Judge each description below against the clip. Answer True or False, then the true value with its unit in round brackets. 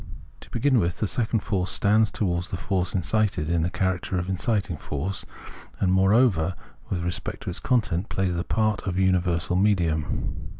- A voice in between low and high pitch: False (95 Hz)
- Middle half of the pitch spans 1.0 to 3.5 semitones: True (3.1 semitones)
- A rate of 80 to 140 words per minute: False (170 wpm)